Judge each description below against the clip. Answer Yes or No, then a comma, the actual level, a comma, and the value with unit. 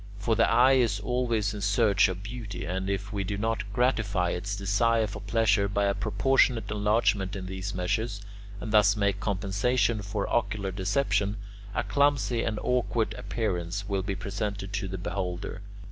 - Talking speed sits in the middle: Yes, average, 165 wpm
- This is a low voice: Yes, low, 105 Hz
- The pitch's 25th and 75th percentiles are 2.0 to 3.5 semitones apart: Yes, narrow, 2.5 semitones